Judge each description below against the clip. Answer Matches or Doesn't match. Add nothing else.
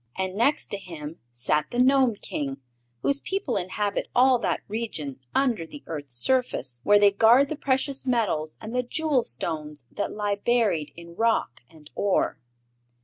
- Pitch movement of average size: Doesn't match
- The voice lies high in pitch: Matches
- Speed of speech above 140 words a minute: Matches